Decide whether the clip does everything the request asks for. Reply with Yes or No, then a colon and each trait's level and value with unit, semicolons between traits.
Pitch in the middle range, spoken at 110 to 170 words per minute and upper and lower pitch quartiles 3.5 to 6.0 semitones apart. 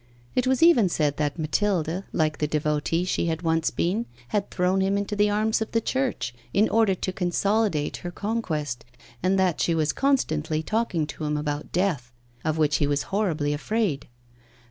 No: medium, 175 Hz; average, 180 wpm; wide, 5.4 semitones